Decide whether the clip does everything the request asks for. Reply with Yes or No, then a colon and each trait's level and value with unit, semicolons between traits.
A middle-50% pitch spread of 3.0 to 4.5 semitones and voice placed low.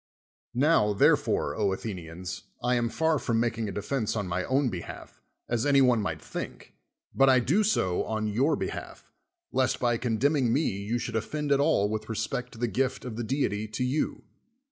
Yes: average, 4.0 semitones; low, 115 Hz